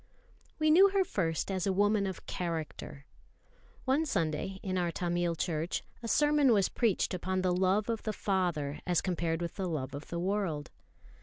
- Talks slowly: No, average, 175 wpm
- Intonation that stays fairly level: No, average, 3.7 semitones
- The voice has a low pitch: No, medium, 185 Hz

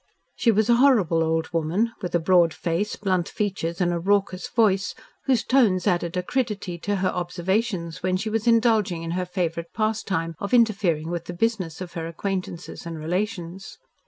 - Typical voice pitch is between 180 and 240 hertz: Yes, medium, 185 Hz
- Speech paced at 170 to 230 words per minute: Yes, average, 175 wpm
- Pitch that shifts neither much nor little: Yes, average, 3.9 semitones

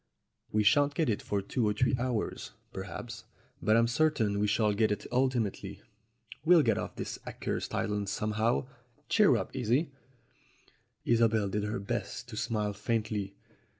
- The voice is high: No, low, 110 Hz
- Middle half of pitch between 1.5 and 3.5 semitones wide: Yes, average, 3.0 semitones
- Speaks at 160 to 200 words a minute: No, average, 150 wpm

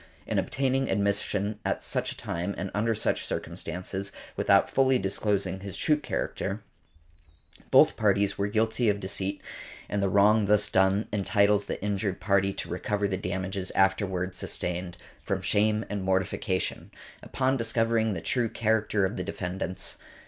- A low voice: Yes, low, 100 Hz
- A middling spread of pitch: No, narrow, 2.1 semitones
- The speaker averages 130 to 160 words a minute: Yes, average, 150 wpm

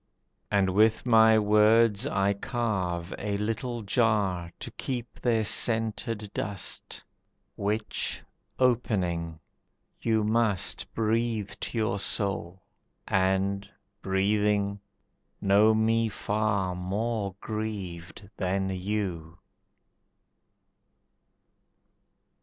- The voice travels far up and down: No, narrow, 2.5 semitones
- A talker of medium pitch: No, low, 105 Hz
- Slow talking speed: Yes, slow, 85 wpm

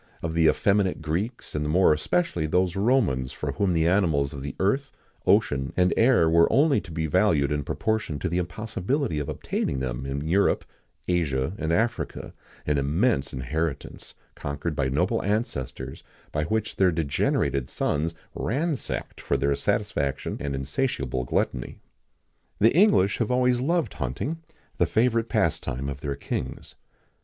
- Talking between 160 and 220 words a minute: No, average, 150 wpm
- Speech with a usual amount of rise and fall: No, wide, 7.6 semitones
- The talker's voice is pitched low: Yes, very low, 85 Hz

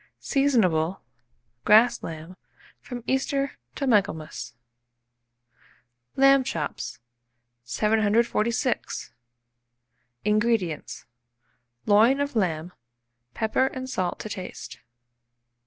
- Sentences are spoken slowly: Yes, slow, 75 wpm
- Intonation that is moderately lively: No, wide, 6.7 semitones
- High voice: Yes, high, 215 Hz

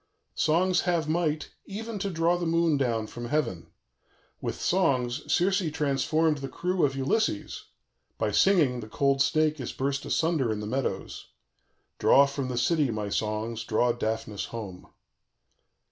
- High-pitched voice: No, medium, 140 Hz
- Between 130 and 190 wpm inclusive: Yes, average, 150 wpm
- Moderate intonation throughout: No, wide, 5.7 semitones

